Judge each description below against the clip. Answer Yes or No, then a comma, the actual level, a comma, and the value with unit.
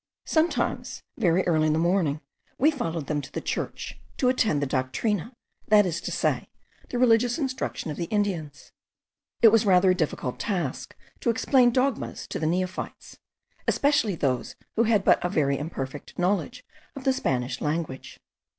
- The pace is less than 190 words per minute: Yes, average, 165 wpm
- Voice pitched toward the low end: No, medium, 185 Hz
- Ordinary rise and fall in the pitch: No, wide, 7.2 semitones